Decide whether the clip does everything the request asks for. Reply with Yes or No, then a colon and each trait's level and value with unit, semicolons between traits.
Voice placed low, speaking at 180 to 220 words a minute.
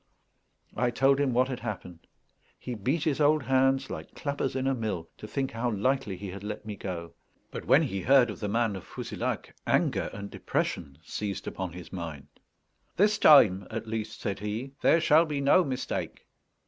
Yes: low, 115 Hz; average, 185 wpm